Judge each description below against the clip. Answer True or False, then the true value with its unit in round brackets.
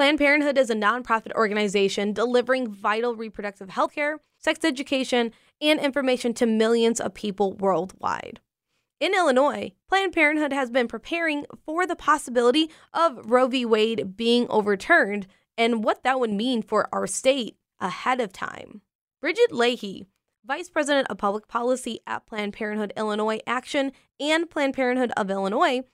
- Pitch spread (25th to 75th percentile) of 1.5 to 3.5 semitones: False (4.9 semitones)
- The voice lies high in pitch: True (245 Hz)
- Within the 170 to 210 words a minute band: False (150 wpm)